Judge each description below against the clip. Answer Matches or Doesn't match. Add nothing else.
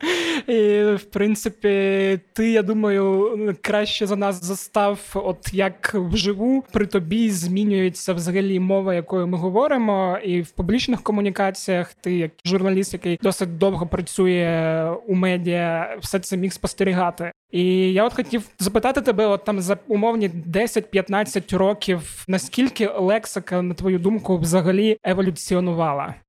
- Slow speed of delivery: Doesn't match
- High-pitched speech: Matches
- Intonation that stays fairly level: Matches